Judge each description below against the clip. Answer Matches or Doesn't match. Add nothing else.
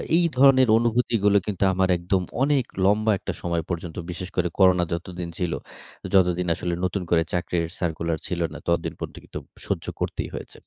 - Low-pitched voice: Matches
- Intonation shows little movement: Doesn't match